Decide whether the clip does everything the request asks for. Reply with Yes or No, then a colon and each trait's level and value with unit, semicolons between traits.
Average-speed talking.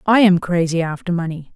Yes: average, 195 wpm